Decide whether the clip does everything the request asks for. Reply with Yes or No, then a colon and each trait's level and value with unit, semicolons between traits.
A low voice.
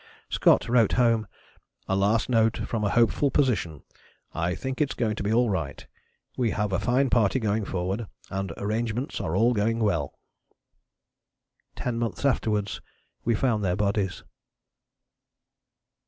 Yes: low, 110 Hz